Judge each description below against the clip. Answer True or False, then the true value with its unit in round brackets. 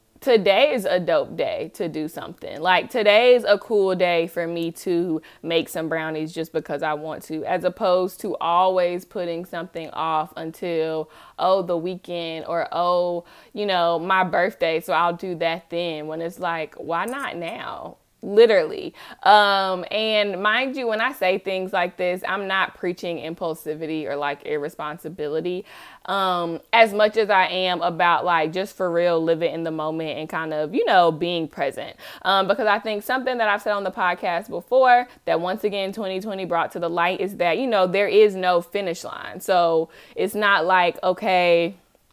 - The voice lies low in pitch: False (175 Hz)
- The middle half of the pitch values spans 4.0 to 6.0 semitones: False (2.8 semitones)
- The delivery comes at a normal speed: True (180 wpm)